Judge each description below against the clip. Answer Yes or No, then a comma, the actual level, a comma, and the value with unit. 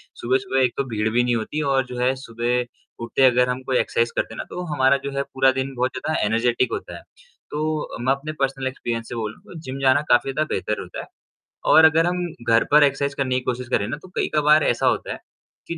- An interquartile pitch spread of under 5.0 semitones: Yes, narrow, 2.5 semitones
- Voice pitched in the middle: No, low, 130 Hz